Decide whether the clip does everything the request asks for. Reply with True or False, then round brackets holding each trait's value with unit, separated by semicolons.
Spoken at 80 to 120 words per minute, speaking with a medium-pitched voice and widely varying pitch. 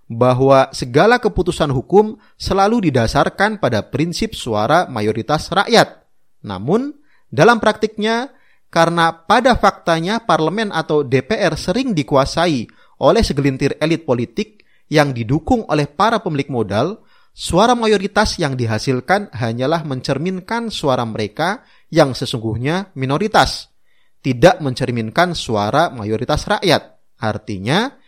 True (105 wpm; 160 Hz; 7.8 semitones)